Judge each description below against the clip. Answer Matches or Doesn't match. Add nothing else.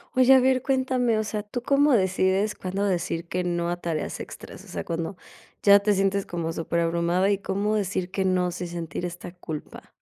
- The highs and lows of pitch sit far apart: Doesn't match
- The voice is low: Doesn't match